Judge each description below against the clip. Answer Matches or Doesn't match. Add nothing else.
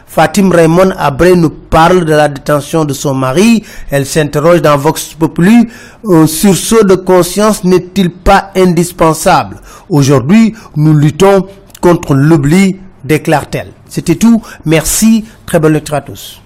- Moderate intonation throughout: Matches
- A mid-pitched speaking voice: Matches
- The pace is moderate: Doesn't match